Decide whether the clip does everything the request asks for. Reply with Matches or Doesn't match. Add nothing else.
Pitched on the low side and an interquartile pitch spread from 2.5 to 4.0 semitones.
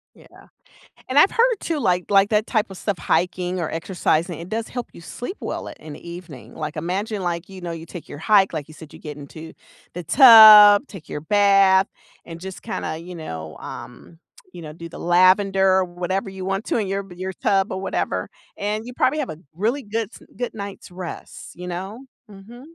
Doesn't match